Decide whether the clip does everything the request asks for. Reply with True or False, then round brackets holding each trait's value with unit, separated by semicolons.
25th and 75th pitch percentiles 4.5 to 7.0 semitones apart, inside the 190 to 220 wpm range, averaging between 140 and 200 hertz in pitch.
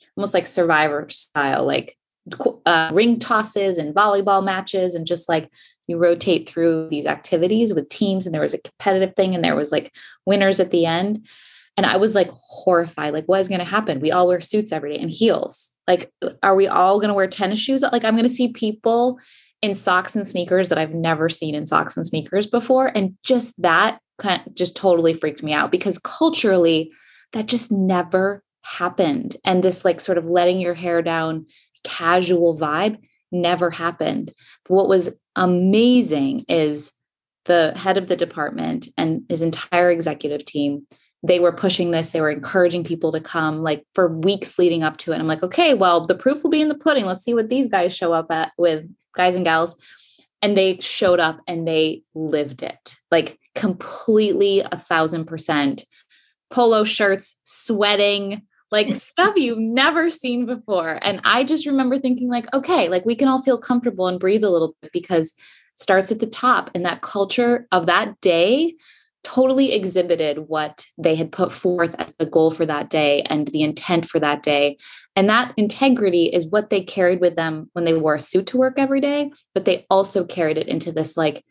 True (4.8 semitones; 195 wpm; 185 Hz)